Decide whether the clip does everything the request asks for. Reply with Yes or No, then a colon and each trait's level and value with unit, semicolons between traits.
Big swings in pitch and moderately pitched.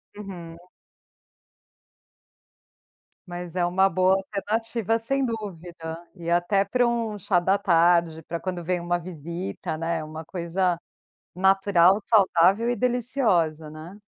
No: average, 3.3 semitones; medium, 180 Hz